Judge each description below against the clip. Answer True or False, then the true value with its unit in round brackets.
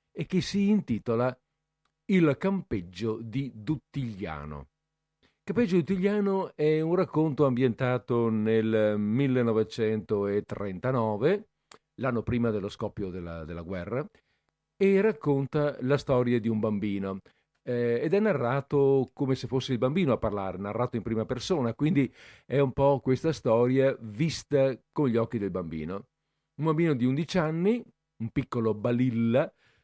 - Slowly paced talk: False (135 wpm)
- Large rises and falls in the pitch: True (5.8 semitones)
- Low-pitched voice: True (130 Hz)